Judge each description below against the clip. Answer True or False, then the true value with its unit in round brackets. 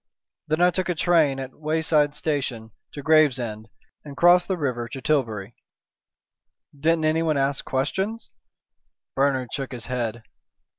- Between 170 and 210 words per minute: False (140 wpm)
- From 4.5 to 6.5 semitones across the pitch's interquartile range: False (3.9 semitones)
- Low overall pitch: False (145 Hz)